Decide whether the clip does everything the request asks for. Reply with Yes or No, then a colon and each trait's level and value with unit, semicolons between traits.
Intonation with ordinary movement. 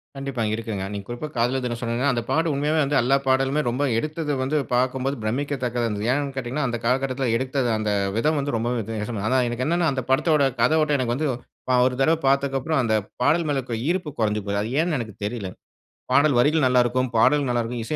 Yes: average, 3.3 semitones